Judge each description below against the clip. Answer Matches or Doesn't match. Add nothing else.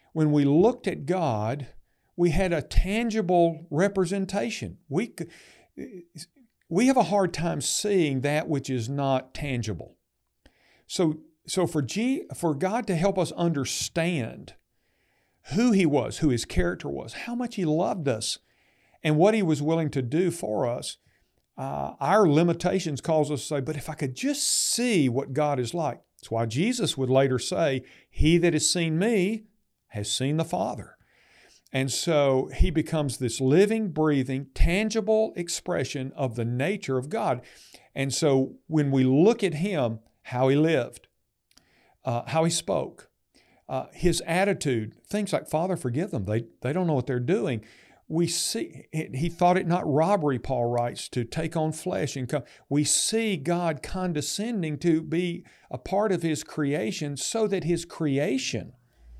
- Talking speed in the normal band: Matches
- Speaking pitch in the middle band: Matches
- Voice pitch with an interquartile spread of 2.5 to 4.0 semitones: Doesn't match